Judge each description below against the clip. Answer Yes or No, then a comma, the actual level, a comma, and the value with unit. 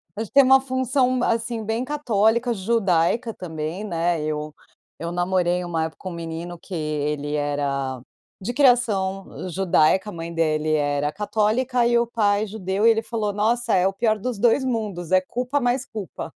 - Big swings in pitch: Yes, wide, 5.9 semitones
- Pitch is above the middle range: Yes, high, 200 Hz